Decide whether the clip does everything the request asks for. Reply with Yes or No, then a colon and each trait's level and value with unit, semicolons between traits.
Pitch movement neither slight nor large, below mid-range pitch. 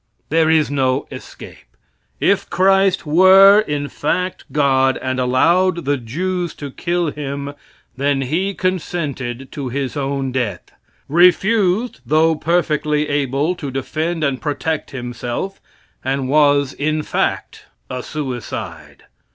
No: average, 4.4 semitones; medium, 145 Hz